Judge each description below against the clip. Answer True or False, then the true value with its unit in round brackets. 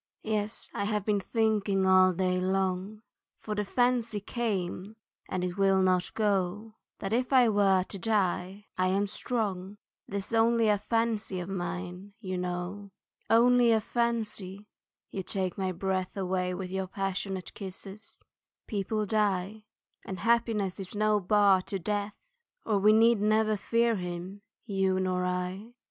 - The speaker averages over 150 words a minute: False (145 wpm)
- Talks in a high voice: True (200 Hz)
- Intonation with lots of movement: False (2.6 semitones)